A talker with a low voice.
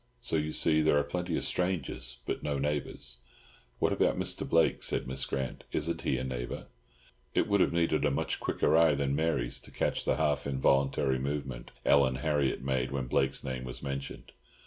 Yes: very low, 70 Hz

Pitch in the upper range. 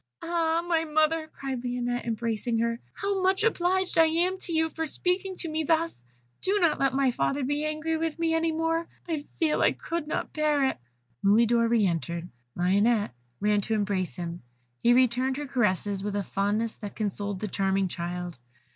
Yes: very high, 265 Hz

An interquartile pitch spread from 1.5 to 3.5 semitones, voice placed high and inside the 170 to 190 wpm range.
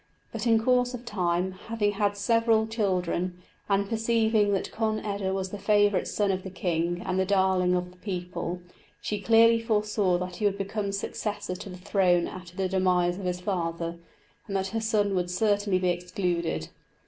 Yes: average, 2.7 semitones; high, 195 Hz; average, 185 wpm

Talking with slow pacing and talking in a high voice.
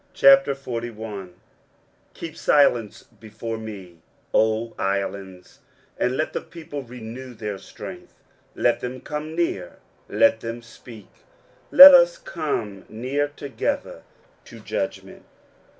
No: slow, 110 wpm; low, 120 Hz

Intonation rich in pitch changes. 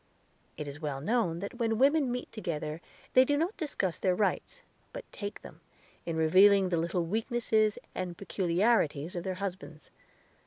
Yes: wide, 5.8 semitones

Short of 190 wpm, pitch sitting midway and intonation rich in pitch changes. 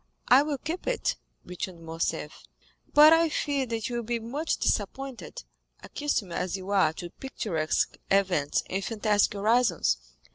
No: average, 145 wpm; high, 220 Hz; wide, 6.6 semitones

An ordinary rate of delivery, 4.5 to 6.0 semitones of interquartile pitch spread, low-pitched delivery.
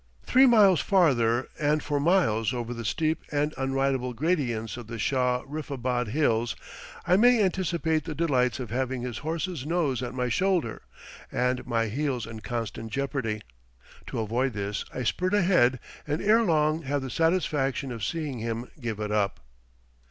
Yes: average, 160 wpm; average, 5.2 semitones; low, 130 Hz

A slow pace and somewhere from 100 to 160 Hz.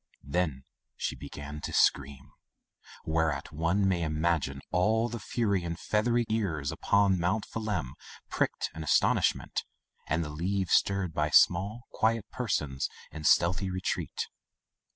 No: slow, 130 wpm; very low, 85 Hz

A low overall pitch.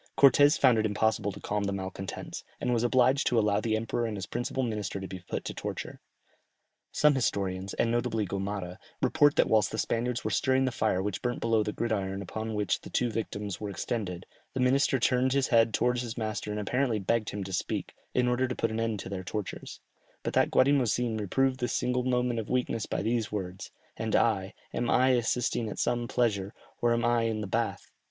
Yes: low, 115 Hz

